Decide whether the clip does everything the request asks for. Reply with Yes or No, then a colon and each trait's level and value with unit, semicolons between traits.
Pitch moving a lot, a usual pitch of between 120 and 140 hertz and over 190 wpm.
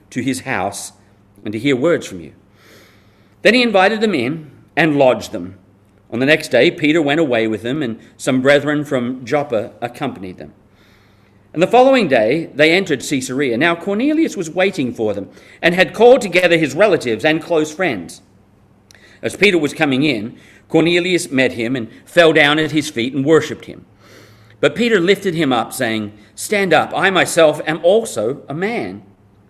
No: wide, 8.3 semitones; low, 135 Hz; average, 175 wpm